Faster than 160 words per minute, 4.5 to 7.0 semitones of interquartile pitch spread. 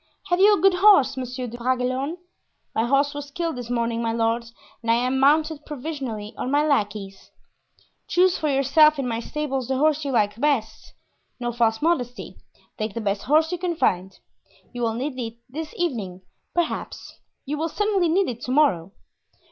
Yes: average, 180 wpm; average, 5.0 semitones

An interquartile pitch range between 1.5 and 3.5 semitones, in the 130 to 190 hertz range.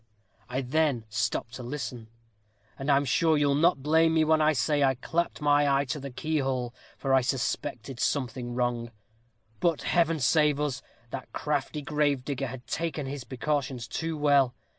Yes: average, 3.0 semitones; medium, 140 Hz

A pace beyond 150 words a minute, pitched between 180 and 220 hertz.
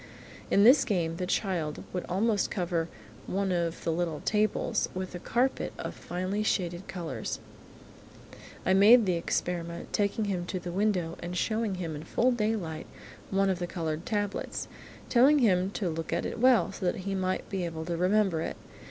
Yes: average, 180 wpm; medium, 185 Hz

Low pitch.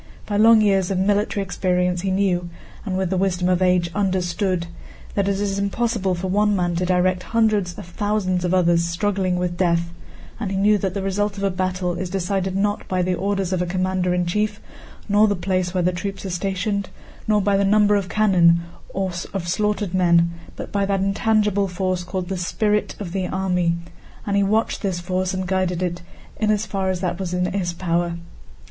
No: high, 190 Hz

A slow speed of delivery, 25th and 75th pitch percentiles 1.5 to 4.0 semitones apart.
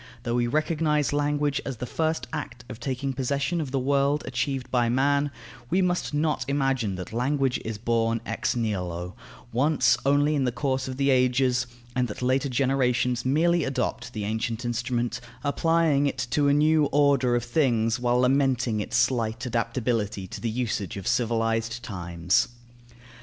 No: average, 165 wpm; average, 3.4 semitones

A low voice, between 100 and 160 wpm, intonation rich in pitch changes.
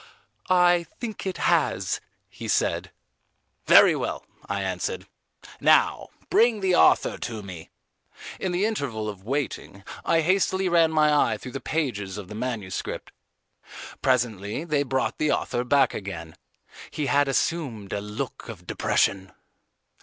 Yes: low, 130 Hz; average, 140 wpm; wide, 8.0 semitones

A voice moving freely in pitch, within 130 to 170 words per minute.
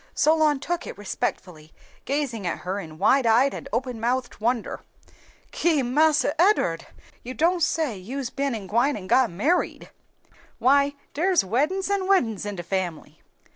Yes: wide, 6.9 semitones; average, 155 wpm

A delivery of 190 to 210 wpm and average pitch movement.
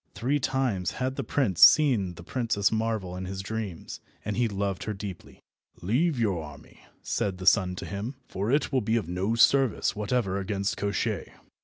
No: average, 180 wpm; average, 4.1 semitones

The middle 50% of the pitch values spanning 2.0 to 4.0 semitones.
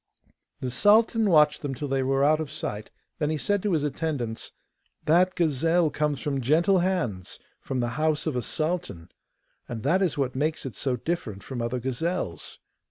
No: average, 5.0 semitones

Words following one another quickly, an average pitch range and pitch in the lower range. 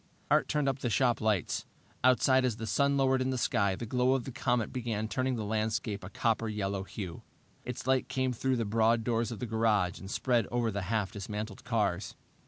Yes: fast, 210 wpm; average, 3.3 semitones; low, 115 Hz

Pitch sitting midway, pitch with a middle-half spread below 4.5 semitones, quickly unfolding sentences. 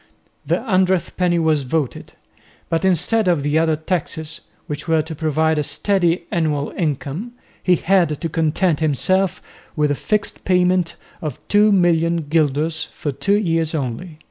No: medium, 165 Hz; average, 3.1 semitones; average, 145 wpm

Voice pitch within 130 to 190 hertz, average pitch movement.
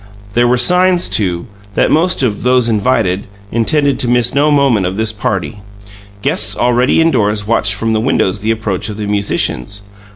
No: low, 110 Hz; average, 3.9 semitones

